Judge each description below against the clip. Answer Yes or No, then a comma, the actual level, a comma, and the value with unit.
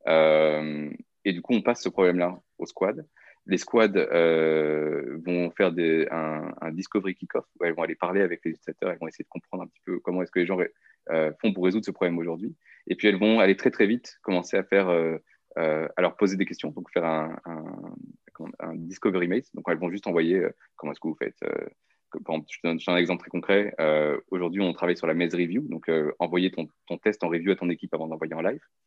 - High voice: No, very low, 85 Hz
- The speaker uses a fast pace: Yes, fast, 245 wpm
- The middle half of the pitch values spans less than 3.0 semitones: Yes, narrow, 2.5 semitones